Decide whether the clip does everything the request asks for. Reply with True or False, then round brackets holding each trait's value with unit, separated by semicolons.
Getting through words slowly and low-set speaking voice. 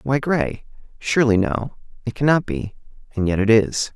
True (120 wpm; 115 Hz)